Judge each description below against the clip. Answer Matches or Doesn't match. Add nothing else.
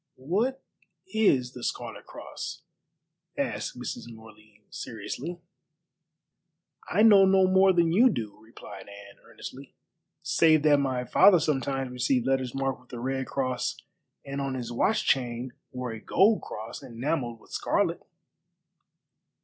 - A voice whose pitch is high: Doesn't match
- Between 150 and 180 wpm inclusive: Doesn't match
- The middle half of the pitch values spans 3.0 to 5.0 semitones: Doesn't match